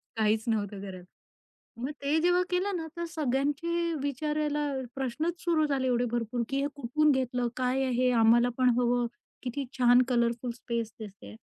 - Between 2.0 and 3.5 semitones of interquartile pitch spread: No, average, 4.1 semitones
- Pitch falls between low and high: No, very high, 255 Hz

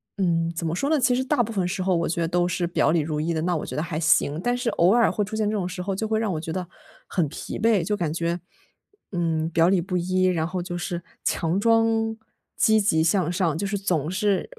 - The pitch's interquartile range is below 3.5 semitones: No, average, 3.8 semitones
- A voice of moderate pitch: Yes, medium, 180 Hz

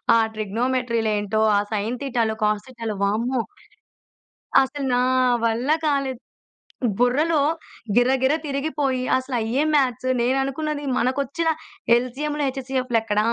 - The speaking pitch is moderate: No, very high, 255 Hz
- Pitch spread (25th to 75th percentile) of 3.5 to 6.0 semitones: No, average, 3.1 semitones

